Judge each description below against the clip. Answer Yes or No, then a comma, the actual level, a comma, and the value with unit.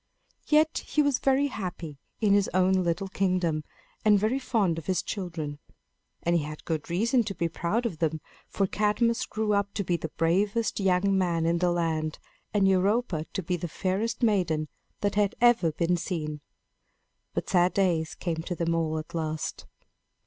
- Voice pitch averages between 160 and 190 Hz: Yes, medium, 185 Hz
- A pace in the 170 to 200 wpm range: Yes, average, 180 wpm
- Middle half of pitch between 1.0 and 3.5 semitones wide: No, average, 3.9 semitones